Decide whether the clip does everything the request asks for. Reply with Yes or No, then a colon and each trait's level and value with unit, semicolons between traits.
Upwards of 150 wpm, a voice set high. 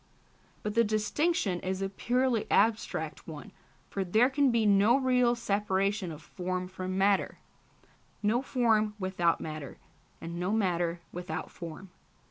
No: slow, 135 wpm; high, 200 Hz